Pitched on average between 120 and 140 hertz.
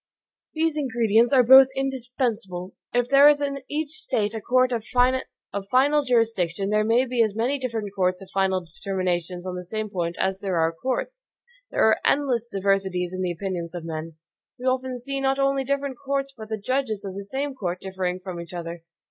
No: high, 225 Hz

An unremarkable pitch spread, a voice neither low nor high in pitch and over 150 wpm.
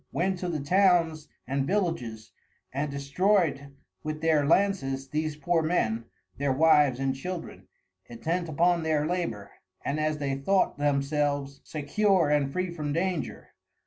No: average, 3.9 semitones; medium, 150 Hz; average, 140 wpm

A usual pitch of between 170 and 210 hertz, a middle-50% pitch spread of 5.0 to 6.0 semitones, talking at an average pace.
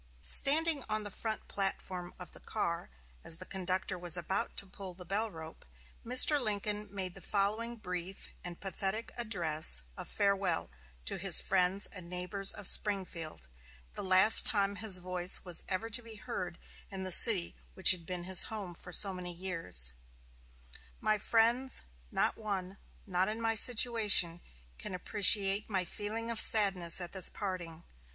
No: high, 190 Hz; average, 3.0 semitones; average, 160 wpm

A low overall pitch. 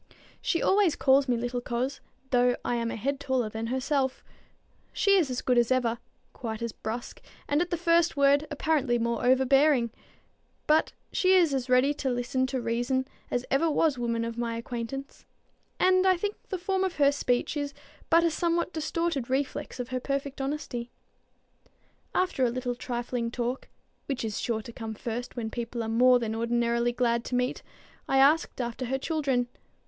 No: very high, 255 Hz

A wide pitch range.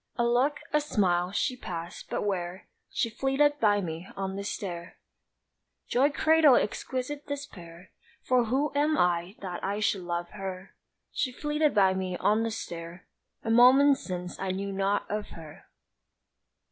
Yes: wide, 6.4 semitones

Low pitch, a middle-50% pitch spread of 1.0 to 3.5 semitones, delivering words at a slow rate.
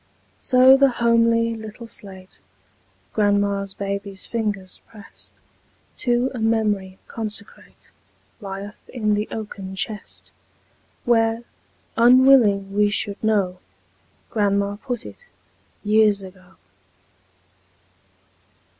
No: high, 210 Hz; narrow, 2.6 semitones; slow, 90 wpm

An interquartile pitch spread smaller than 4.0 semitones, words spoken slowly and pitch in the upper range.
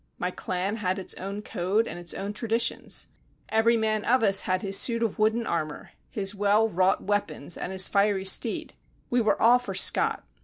No: average, 2.9 semitones; average, 190 wpm; high, 205 Hz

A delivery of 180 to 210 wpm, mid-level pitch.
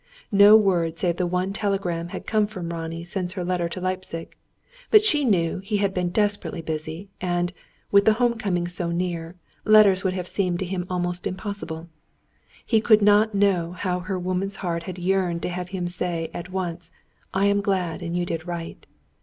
Yes: average, 190 wpm; medium, 180 Hz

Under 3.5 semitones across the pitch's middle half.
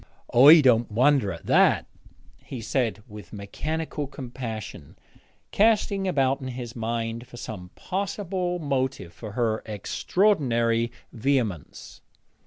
No: average, 4.8 semitones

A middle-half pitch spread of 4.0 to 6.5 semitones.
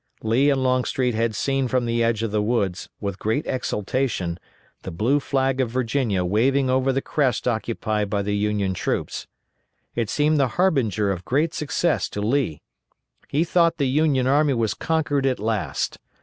Yes: average, 4.4 semitones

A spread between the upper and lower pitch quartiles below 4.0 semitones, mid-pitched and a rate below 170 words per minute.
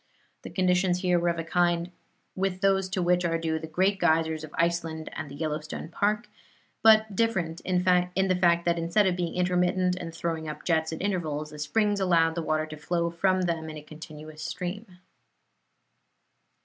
No: narrow, 2.4 semitones; medium, 175 Hz; average, 185 wpm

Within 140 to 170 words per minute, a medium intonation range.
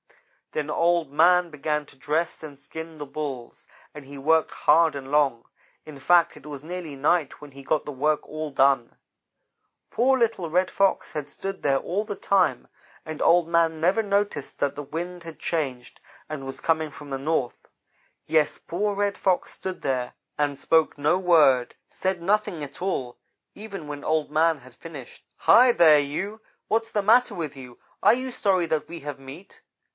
No: average, 180 wpm; average, 4.0 semitones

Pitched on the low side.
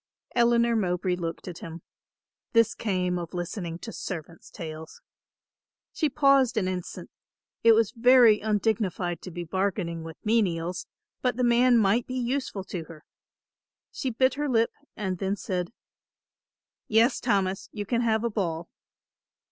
No: high, 200 Hz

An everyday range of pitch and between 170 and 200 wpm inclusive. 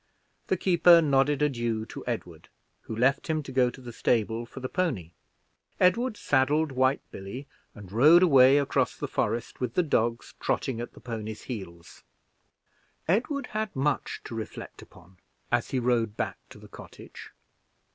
No: average, 4.6 semitones; average, 160 wpm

